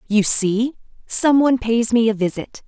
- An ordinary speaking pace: Yes, average, 180 wpm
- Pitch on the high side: Yes, high, 230 Hz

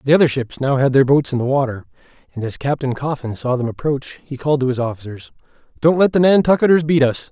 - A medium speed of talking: No, fast, 230 wpm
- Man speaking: Yes, male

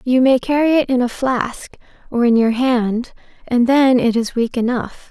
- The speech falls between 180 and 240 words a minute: Yes, average, 200 wpm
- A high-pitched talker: Yes, high, 245 Hz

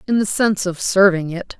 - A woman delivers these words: Yes, female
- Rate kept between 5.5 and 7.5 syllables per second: Yes, 5.6 syllables/s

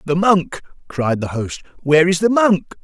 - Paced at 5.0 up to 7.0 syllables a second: No, 4.7 syllables/s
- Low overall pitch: No, medium, 170 Hz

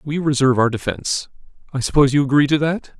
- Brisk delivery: No, average, 180 wpm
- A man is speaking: Yes, male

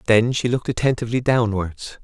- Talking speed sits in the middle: Yes, average, 145 wpm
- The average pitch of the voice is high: No, low, 115 Hz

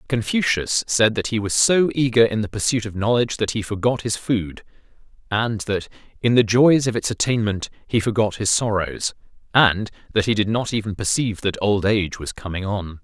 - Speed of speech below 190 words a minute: No, average, 195 wpm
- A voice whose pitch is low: Yes, low, 110 Hz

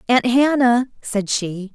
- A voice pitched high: Yes, high, 235 Hz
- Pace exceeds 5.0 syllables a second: No, 3.5 syllables/s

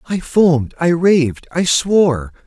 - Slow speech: Yes, slow, 95 wpm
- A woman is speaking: No, male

